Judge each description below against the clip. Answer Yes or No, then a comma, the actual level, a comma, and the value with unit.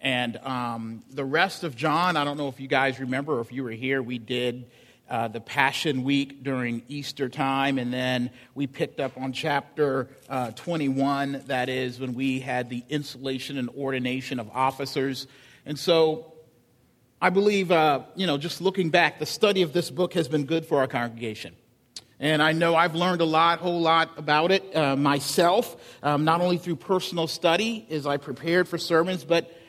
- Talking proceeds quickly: No, average, 190 wpm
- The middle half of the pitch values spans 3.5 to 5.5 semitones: Yes, average, 4.1 semitones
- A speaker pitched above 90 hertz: Yes, medium, 140 Hz